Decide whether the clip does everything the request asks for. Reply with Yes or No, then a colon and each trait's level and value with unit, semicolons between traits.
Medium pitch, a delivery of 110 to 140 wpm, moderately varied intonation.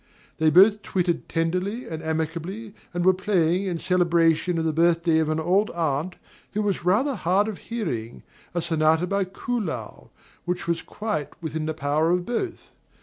No: medium, 175 Hz; average, 165 wpm; average, 3.5 semitones